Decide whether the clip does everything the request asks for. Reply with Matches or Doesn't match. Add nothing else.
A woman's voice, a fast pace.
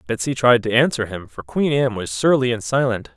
Doesn't match